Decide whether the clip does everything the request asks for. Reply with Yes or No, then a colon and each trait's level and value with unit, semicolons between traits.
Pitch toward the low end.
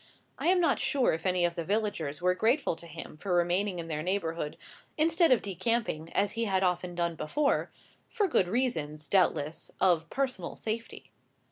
No: medium, 185 Hz